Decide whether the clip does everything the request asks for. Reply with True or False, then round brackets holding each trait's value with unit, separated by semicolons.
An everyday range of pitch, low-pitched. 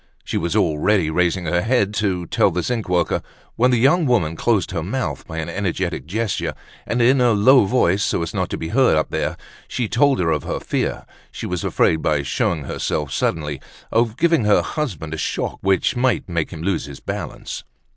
False (6.5 semitones; 95 Hz)